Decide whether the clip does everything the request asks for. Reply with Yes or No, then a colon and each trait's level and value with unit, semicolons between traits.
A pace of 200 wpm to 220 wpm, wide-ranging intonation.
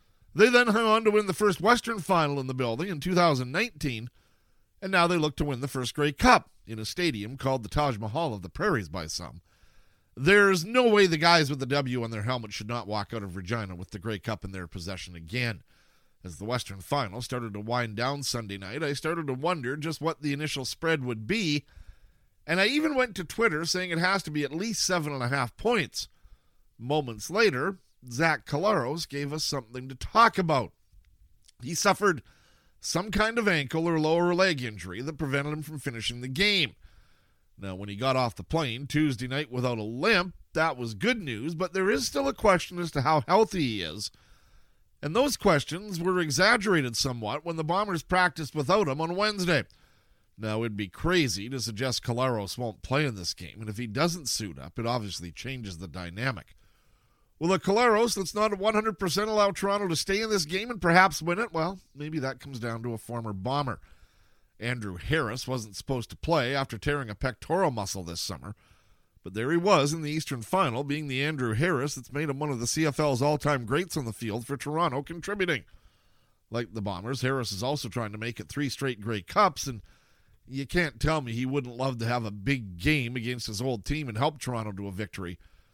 Yes: fast, 205 wpm; wide, 7.3 semitones